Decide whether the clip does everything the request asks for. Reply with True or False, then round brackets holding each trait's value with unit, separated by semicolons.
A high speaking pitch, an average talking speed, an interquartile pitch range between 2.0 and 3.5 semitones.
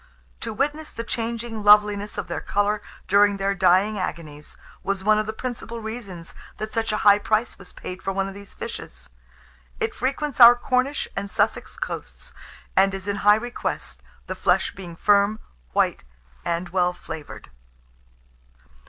True (205 Hz; 160 wpm; 2.9 semitones)